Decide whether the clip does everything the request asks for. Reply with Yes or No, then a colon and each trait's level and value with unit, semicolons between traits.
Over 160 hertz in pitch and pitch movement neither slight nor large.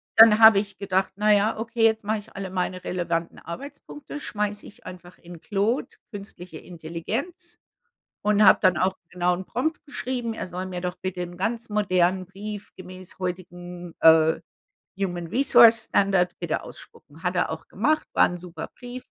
Yes: high, 190 Hz; average, 3.7 semitones